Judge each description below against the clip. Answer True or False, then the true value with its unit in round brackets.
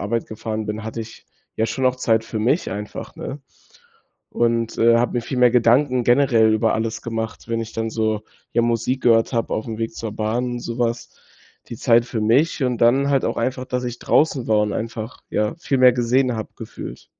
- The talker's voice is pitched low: True (115 Hz)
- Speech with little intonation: True (2.0 semitones)